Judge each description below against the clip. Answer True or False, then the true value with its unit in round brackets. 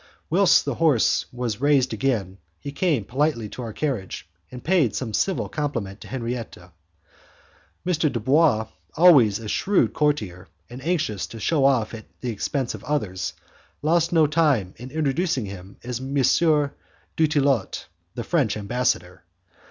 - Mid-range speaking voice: False (125 Hz)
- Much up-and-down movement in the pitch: True (5.9 semitones)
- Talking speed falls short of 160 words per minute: True (145 wpm)